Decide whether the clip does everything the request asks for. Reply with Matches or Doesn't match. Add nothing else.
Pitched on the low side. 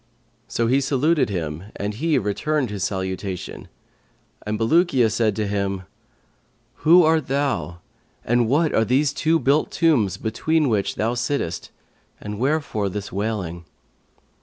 Matches